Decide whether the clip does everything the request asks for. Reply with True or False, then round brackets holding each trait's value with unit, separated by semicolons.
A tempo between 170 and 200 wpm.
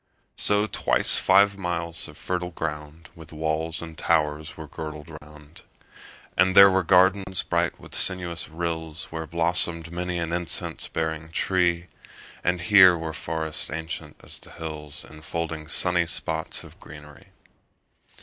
False (145 wpm)